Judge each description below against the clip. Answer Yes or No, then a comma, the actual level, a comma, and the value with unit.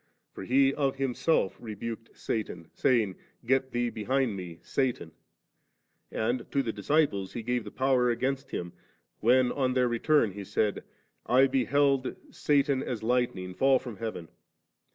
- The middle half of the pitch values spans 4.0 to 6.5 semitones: No, average, 3.6 semitones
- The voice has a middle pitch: No, low, 125 Hz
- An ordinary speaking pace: Yes, average, 160 wpm